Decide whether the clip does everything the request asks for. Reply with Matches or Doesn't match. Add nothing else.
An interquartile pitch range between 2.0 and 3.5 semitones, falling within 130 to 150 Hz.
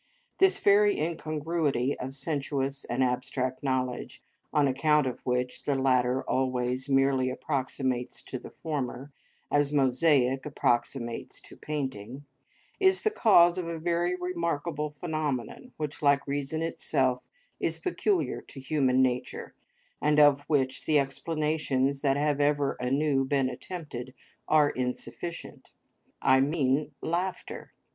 Matches